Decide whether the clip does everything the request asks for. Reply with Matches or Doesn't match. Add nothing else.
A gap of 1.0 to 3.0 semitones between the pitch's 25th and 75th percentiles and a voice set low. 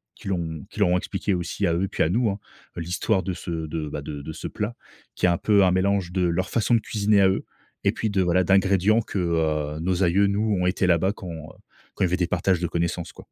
Matches